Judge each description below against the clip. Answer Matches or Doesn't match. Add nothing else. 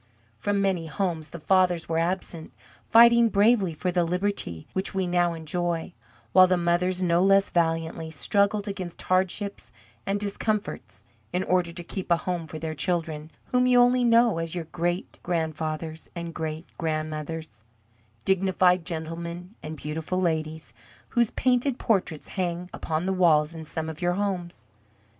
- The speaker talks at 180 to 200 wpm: Doesn't match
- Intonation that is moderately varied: Matches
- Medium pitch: Matches